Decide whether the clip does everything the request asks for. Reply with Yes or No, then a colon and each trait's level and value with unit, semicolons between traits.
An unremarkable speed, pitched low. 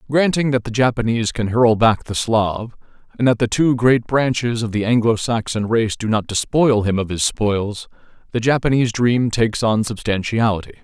Yes: average, 185 wpm; low, 115 Hz